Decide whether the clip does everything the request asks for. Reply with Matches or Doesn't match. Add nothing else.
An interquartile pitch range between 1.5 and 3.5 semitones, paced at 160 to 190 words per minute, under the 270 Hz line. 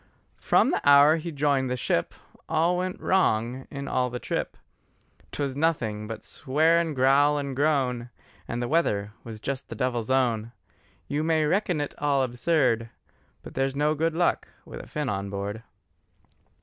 Doesn't match